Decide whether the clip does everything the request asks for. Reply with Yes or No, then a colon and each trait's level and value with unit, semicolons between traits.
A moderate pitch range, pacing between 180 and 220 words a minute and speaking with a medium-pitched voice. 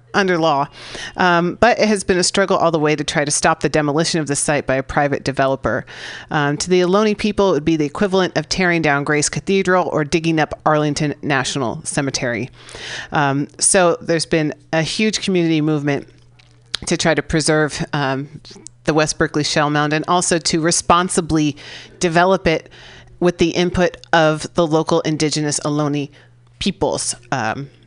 No: average, 3.4 semitones; average, 170 wpm; medium, 155 Hz